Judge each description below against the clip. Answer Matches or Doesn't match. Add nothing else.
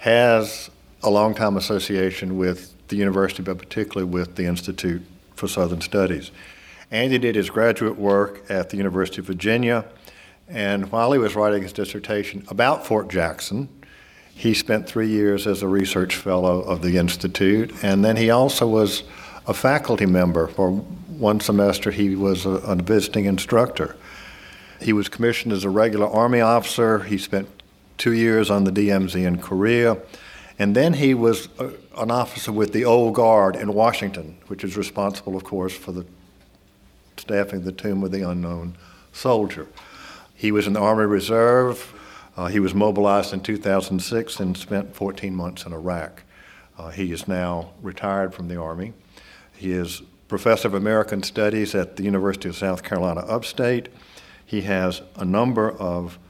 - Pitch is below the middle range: Matches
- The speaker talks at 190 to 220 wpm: Doesn't match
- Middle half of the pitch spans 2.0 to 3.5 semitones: Matches